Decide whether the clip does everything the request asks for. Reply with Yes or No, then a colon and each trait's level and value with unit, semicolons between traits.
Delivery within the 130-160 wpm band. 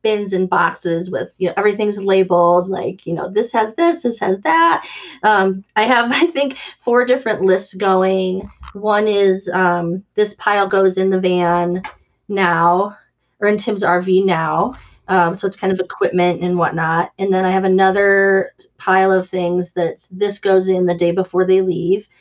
No: average, 180 wpm